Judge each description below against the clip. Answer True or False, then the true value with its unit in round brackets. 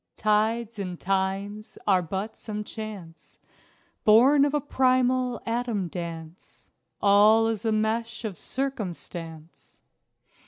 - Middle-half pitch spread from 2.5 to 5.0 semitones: True (3.5 semitones)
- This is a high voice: True (215 Hz)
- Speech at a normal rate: False (110 wpm)